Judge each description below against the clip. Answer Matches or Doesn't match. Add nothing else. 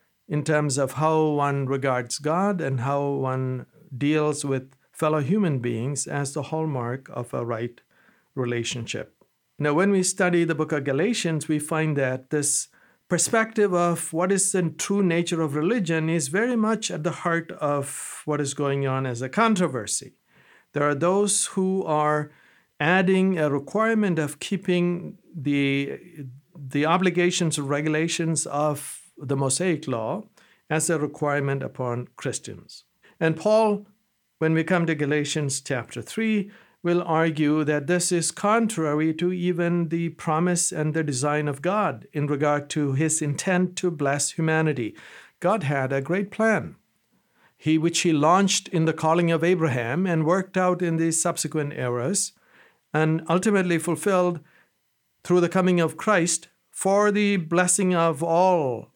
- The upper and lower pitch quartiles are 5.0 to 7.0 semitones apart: Doesn't match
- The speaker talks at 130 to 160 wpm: Matches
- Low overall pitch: Doesn't match